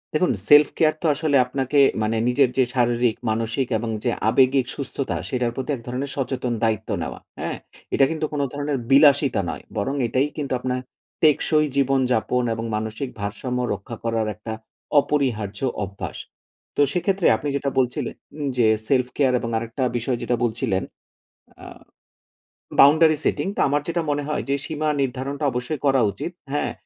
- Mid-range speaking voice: No, low, 130 Hz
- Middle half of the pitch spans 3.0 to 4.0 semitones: Yes, average, 3.4 semitones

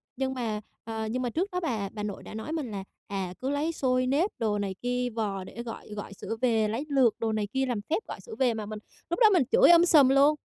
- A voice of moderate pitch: No, high, 245 Hz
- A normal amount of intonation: Yes, average, 4.7 semitones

